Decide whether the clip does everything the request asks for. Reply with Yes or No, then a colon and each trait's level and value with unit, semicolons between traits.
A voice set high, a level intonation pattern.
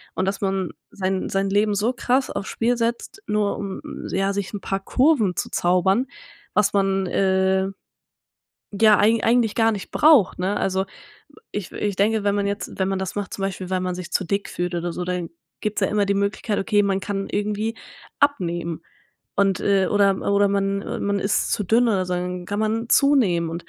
Yes: high, 200 Hz; narrow, 1.9 semitones